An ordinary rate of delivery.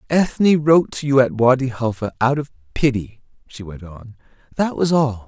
Yes: average, 180 wpm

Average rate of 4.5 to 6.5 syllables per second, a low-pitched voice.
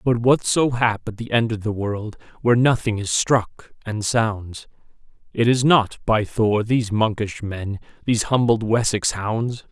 No: 4.2 syllables/s; low, 110 Hz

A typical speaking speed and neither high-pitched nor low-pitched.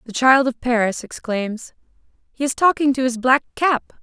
No: average, 180 wpm; very high, 255 Hz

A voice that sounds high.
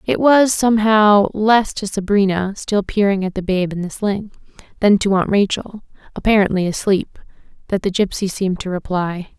Yes: high, 200 Hz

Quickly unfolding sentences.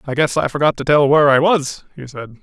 Yes: fast, 270 wpm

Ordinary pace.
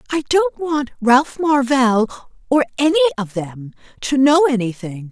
No: slow, 115 wpm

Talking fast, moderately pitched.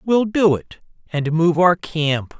No: average, 175 wpm; medium, 170 Hz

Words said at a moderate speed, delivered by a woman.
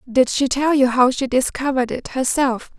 Yes: average, 195 wpm; female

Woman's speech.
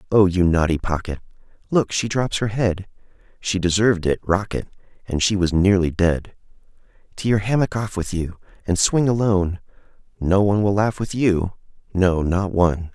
No: male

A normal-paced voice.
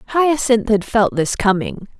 Yes: average, 150 wpm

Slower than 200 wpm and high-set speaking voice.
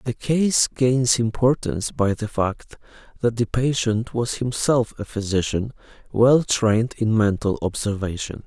No: slow, 135 wpm; low, 115 Hz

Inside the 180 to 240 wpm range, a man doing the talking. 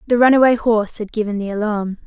No: fast, 205 wpm; female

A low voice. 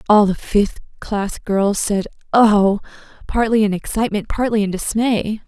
No: high, 210 Hz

